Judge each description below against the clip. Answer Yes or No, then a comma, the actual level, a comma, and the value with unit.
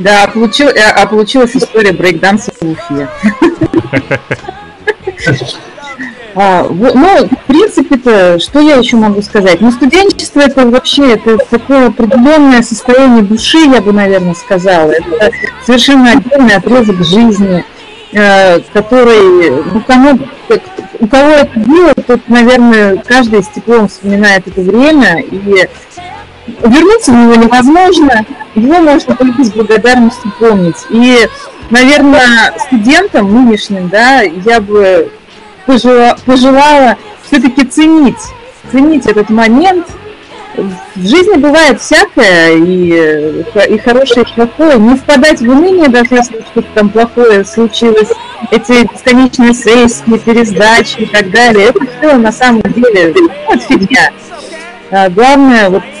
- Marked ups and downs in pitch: No, average, 4.7 semitones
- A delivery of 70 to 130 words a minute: Yes, average, 115 wpm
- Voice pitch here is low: No, high, 240 Hz